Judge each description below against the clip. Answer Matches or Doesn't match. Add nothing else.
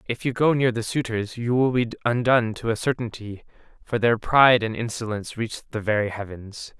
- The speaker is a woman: Doesn't match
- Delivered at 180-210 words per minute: Matches